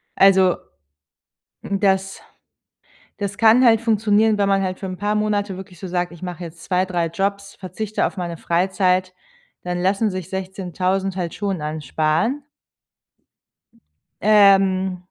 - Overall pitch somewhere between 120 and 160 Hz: No, high, 190 Hz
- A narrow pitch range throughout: Yes, narrow, 2.0 semitones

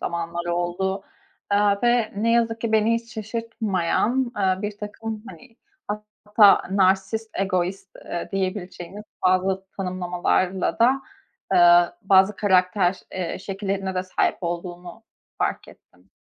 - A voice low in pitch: No, high, 195 Hz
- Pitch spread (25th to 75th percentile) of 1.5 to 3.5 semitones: Yes, average, 2.9 semitones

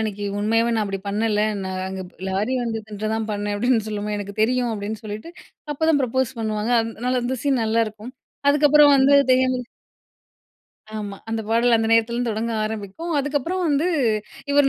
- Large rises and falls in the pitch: No, average, 3.5 semitones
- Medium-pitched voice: No, high, 225 Hz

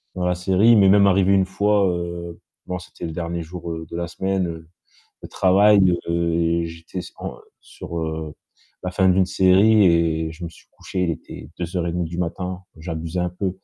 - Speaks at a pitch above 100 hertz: No, very low, 90 Hz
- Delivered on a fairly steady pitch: Yes, narrow, 2.0 semitones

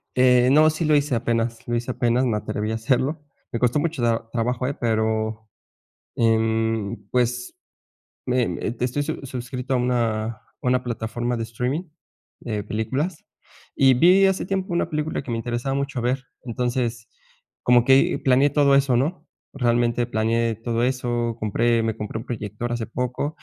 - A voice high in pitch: No, low, 120 Hz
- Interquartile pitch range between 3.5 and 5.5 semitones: No, average, 2.7 semitones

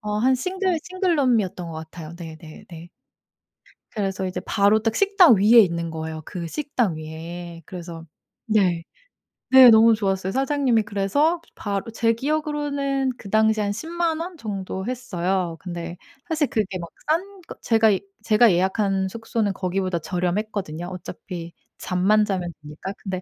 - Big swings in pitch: Yes, wide, 6.0 semitones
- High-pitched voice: Yes, high, 205 Hz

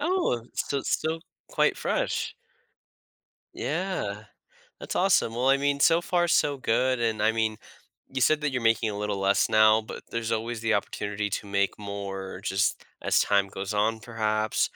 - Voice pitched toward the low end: Yes, low, 110 Hz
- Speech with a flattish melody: No, average, 4.5 semitones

